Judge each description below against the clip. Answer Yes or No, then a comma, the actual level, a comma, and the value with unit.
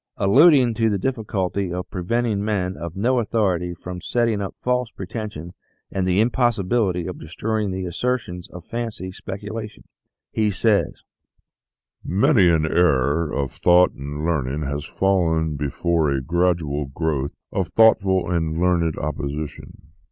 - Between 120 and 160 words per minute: Yes, average, 140 wpm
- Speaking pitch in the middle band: No, very low, 90 Hz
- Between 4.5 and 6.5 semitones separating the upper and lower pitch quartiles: Yes, average, 5.0 semitones